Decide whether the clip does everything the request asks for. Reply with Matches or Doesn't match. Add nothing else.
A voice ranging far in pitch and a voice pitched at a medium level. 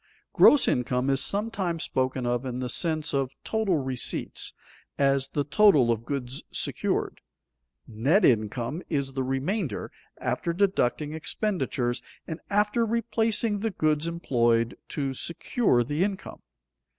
Matches